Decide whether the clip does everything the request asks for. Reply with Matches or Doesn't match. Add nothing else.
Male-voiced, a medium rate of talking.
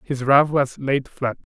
Matches